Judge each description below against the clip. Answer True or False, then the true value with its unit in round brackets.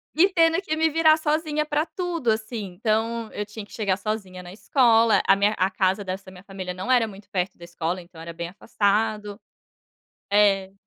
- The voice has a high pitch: True (210 Hz)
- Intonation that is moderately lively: True (5.0 semitones)